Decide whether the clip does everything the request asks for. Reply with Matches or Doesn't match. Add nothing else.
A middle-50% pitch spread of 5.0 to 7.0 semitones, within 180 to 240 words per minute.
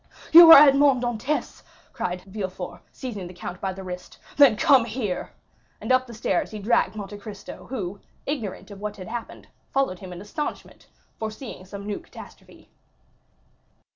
Doesn't match